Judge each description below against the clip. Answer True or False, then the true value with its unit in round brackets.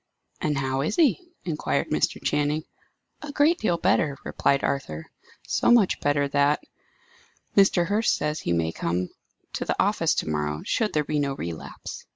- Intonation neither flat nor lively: False (6.7 semitones)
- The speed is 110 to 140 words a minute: False (165 wpm)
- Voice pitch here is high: False (150 Hz)